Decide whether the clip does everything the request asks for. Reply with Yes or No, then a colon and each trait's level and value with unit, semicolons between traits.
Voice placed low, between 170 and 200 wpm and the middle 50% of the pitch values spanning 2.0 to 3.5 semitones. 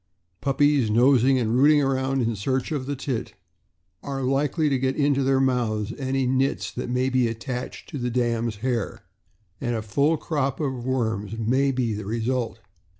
Yes: low, 130 Hz; average, 175 wpm; average, 2.7 semitones